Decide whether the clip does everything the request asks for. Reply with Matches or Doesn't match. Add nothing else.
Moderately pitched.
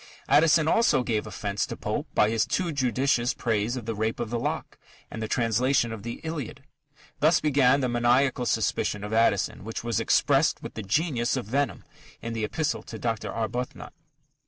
Doesn't match